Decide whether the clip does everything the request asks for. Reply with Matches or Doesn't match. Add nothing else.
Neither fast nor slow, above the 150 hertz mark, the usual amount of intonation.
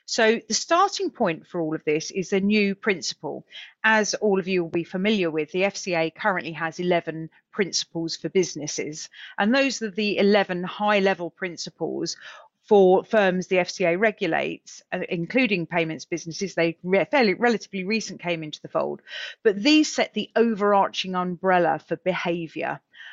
Matches